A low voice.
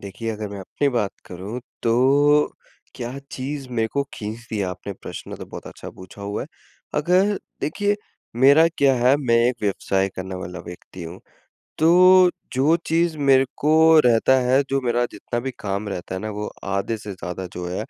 Yes: low, 120 Hz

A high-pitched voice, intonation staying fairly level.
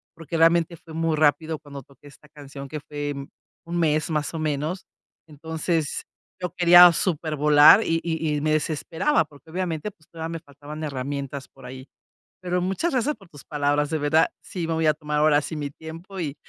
No: medium, 155 Hz; narrow, 2.2 semitones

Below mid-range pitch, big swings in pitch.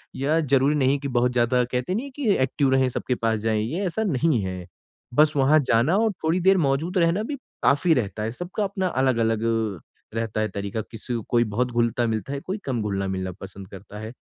Yes: low, 125 Hz; wide, 6.2 semitones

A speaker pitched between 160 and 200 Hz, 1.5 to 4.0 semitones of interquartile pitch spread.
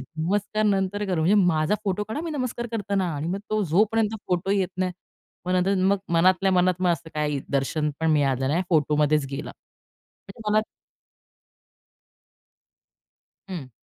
No: medium, 185 Hz; average, 4.7 semitones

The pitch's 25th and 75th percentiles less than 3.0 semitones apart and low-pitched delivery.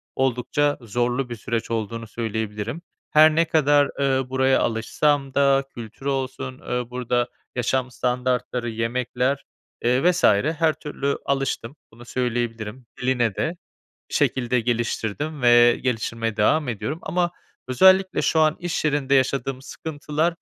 No: average, 3.4 semitones; low, 130 Hz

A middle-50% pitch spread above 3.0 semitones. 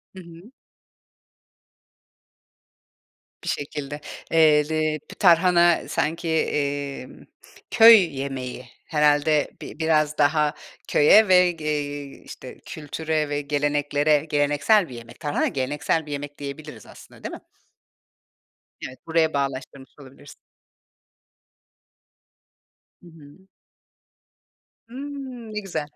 No: narrow, 2.5 semitones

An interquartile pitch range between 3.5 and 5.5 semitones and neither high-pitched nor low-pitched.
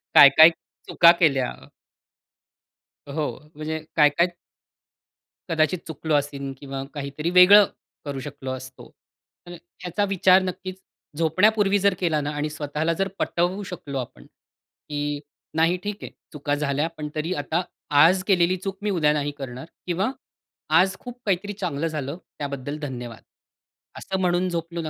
Yes: average, 4.1 semitones; medium, 160 Hz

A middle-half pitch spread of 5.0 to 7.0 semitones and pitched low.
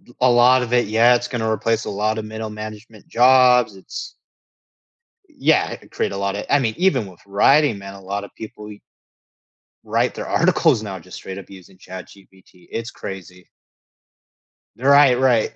No: average, 3.9 semitones; low, 110 Hz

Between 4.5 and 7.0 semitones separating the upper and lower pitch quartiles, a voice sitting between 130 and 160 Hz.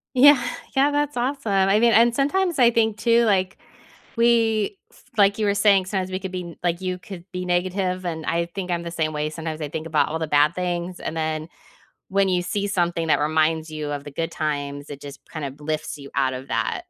No: average, 4.8 semitones; medium, 180 Hz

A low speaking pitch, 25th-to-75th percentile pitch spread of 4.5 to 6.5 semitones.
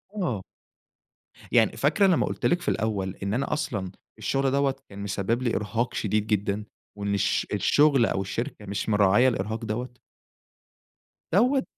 Yes: low, 110 Hz; average, 5.1 semitones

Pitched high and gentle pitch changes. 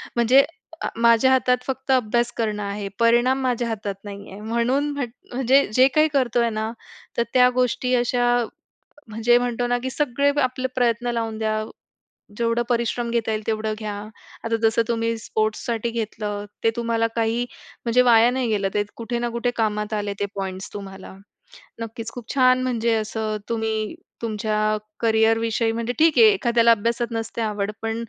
Yes: high, 230 Hz; narrow, 2.0 semitones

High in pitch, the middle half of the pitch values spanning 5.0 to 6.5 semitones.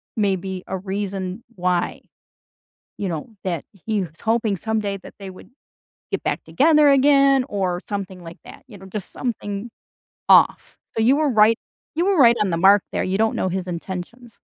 No: high, 200 Hz; average, 3.8 semitones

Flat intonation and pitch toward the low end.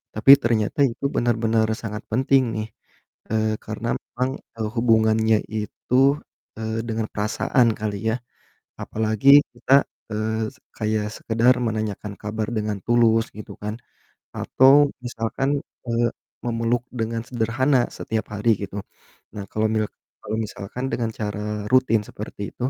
Yes: narrow, 1.7 semitones; low, 110 Hz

